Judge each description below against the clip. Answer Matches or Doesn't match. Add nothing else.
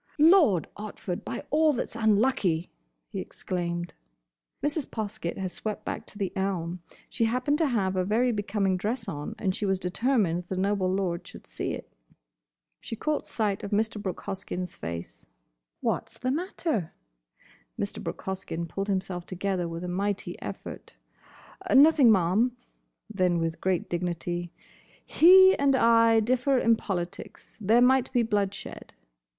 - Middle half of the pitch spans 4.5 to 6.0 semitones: Matches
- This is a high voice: Matches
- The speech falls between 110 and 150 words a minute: Matches